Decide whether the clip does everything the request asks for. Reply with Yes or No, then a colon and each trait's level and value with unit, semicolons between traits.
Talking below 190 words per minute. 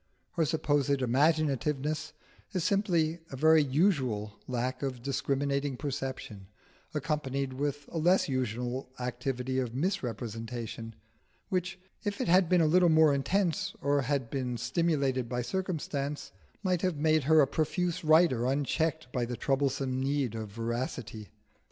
Yes: slow, 135 wpm